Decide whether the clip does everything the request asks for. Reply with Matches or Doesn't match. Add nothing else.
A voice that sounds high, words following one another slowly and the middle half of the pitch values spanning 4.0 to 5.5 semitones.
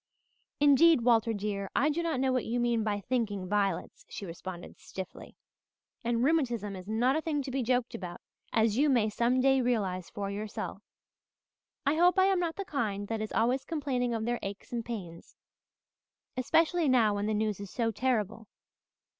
Doesn't match